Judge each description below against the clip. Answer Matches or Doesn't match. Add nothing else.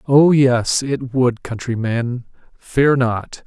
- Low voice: Matches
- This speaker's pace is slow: Matches